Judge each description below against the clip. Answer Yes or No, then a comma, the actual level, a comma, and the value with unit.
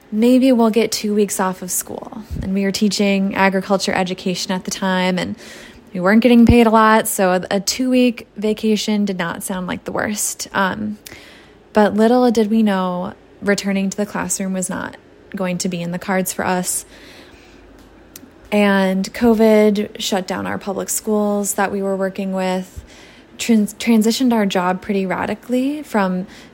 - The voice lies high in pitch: Yes, high, 200 Hz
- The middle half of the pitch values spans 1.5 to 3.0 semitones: Yes, narrow, 2.6 semitones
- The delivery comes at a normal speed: Yes, average, 165 wpm